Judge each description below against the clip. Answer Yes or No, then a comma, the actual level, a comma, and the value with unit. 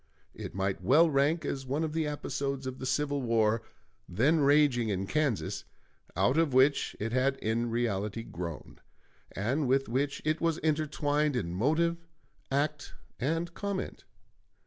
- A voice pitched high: No, low, 135 Hz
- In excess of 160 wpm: No, average, 145 wpm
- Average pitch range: Yes, average, 4.7 semitones